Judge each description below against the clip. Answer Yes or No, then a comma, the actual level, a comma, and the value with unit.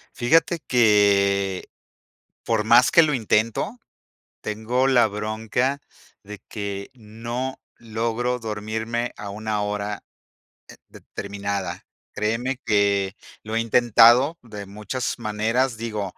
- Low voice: Yes, low, 110 Hz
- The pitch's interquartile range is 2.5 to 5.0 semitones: Yes, average, 2.8 semitones